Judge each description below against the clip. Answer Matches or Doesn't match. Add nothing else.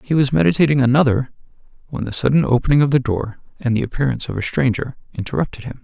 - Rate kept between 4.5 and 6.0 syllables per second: Doesn't match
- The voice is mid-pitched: Doesn't match